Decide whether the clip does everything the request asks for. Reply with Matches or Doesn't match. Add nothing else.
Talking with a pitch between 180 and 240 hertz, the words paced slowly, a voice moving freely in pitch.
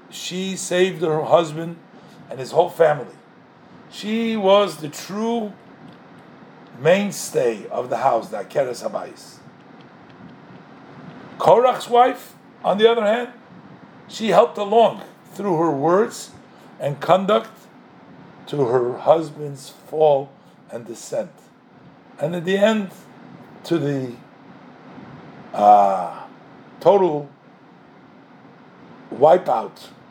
Matches